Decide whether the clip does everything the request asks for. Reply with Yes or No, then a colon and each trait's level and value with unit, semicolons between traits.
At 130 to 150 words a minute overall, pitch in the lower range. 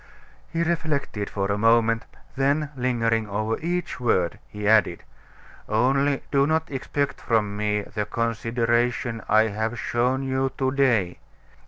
Yes: average, 140 wpm; low, 115 Hz